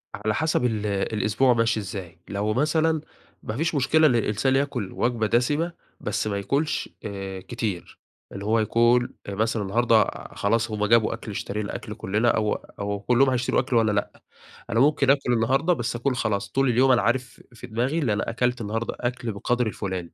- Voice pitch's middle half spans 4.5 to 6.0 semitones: No, average, 3.3 semitones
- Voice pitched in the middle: No, low, 115 Hz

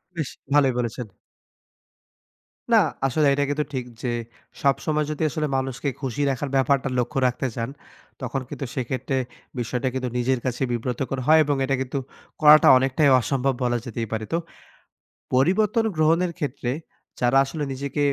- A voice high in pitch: No, low, 135 Hz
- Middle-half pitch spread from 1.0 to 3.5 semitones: Yes, average, 2.8 semitones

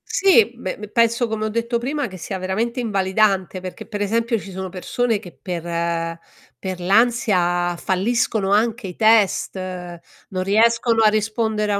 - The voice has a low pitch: No, high, 210 Hz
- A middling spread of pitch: Yes, average, 3.7 semitones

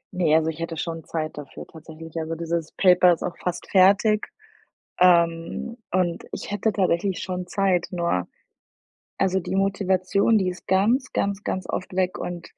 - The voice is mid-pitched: Yes, medium, 180 Hz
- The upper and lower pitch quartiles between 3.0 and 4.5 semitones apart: No, narrow, 2.4 semitones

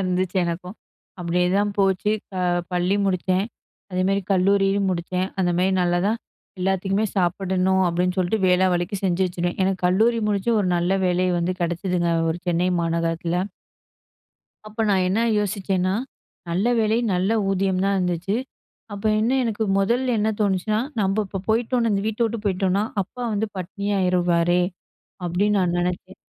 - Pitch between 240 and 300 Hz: No, high, 190 Hz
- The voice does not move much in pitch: Yes, narrow, 2.0 semitones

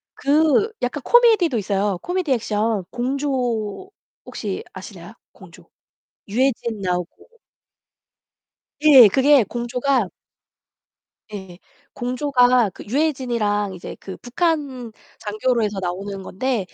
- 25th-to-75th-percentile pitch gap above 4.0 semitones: Yes, average, 5.1 semitones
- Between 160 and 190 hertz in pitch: No, high, 245 Hz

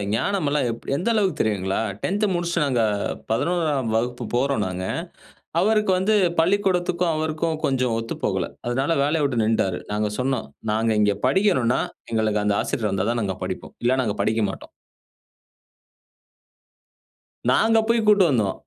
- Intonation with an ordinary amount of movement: No, wide, 7.8 semitones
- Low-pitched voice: Yes, low, 130 Hz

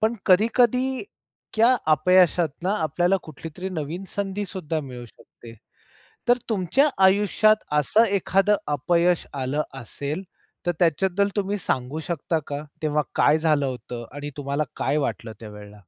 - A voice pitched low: No, medium, 165 Hz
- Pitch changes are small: No, wide, 5.4 semitones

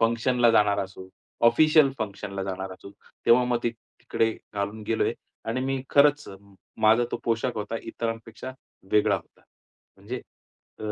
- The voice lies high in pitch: No, low, 115 Hz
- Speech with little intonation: No, average, 3.1 semitones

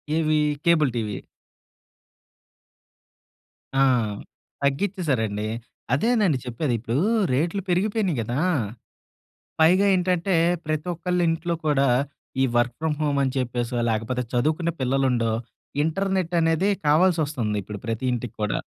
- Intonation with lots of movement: Yes, wide, 6.0 semitones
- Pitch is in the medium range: Yes, medium, 150 Hz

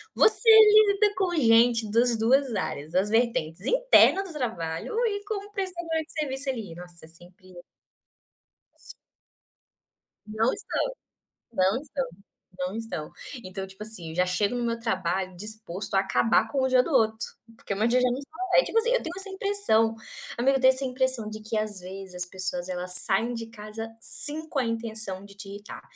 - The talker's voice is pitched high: Yes, high, 225 Hz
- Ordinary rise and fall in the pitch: No, wide, 6.3 semitones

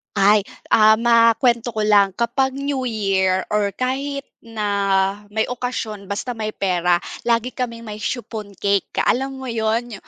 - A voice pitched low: No, high, 220 Hz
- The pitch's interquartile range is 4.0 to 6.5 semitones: No, average, 3.1 semitones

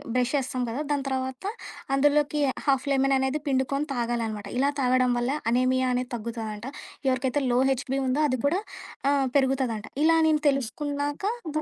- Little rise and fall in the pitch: Yes, narrow, 2.3 semitones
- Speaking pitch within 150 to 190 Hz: No, very high, 265 Hz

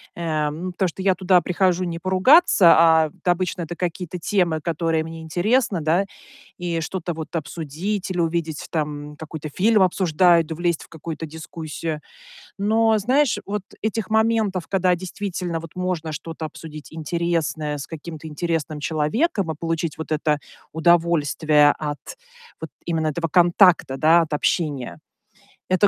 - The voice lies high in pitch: No, medium, 165 Hz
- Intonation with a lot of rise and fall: No, average, 2.7 semitones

